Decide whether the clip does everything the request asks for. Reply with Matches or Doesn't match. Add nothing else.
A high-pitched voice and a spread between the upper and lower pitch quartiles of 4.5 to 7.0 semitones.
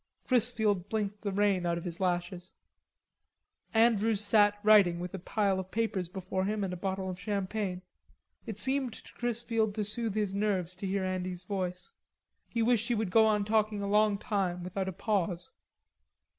Doesn't match